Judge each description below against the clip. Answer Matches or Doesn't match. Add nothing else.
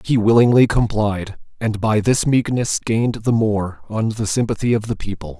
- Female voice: Doesn't match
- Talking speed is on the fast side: Doesn't match